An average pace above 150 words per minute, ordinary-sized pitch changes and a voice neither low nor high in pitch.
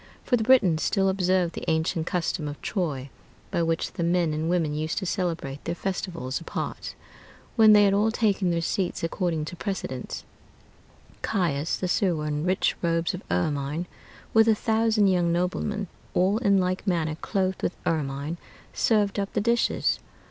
Yes: average, 165 wpm; average, 3.8 semitones; medium, 180 Hz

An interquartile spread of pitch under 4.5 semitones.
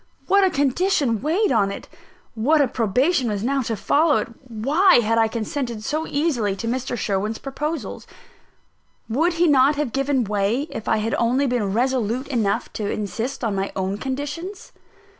No: average, 4.9 semitones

